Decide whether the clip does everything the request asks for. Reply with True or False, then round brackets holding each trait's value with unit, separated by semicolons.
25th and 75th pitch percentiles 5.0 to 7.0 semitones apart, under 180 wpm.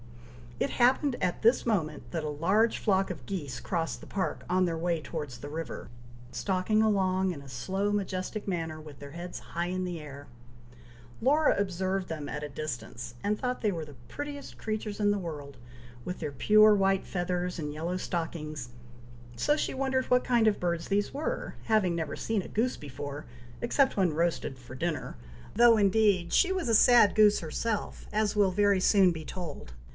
False (5.4 semitones; 185 wpm)